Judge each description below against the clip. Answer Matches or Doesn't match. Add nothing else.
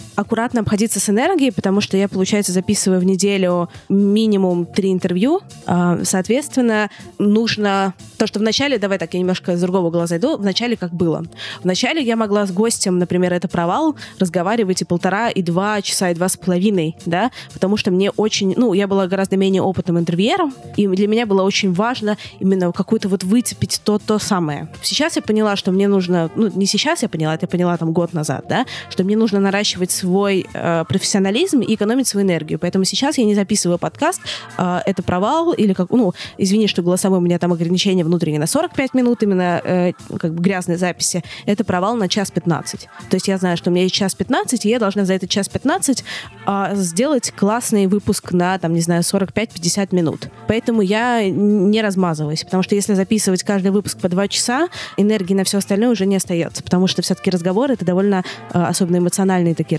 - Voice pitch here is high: Matches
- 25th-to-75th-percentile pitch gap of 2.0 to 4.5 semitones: Matches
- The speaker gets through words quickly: Matches